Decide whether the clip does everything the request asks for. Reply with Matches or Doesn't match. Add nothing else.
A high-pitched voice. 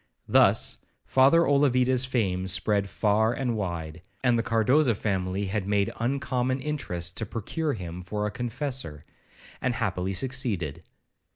Doesn't match